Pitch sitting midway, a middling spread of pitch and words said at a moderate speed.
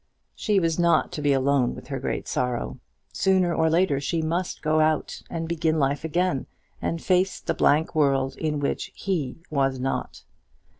Yes: medium, 155 Hz; average, 3.7 semitones; average, 170 wpm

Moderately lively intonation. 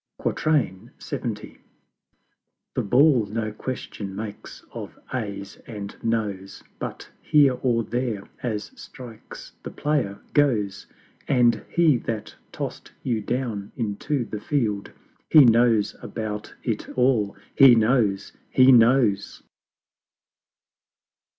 Yes: average, 3.7 semitones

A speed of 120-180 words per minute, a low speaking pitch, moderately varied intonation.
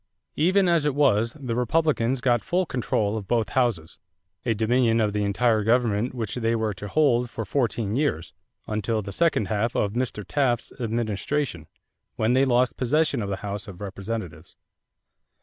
Yes: average, 165 wpm; low, 115 Hz; average, 3.7 semitones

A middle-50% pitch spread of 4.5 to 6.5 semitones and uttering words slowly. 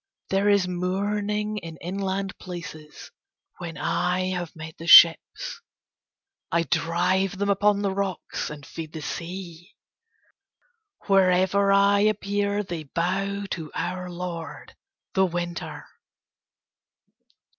No: average, 2.7 semitones; slow, 110 wpm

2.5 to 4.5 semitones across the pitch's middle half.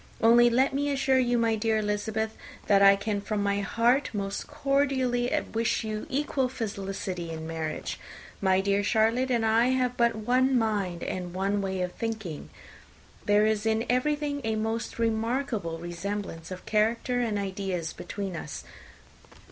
Yes: average, 3.6 semitones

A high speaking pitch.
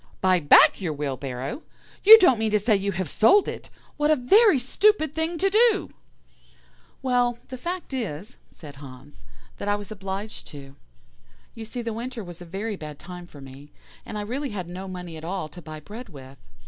Yes: high, 205 Hz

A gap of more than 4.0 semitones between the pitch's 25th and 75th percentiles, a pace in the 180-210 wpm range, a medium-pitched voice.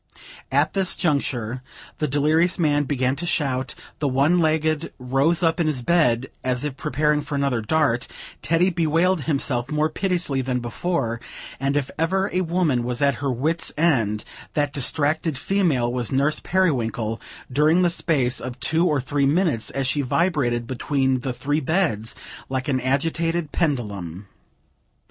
No: average, 4.4 semitones; average, 155 wpm; medium, 145 Hz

